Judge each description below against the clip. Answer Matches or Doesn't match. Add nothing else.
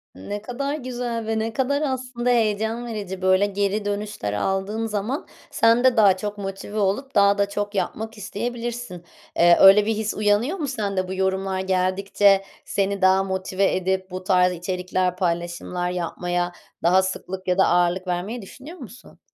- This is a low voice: Doesn't match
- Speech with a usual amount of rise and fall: Matches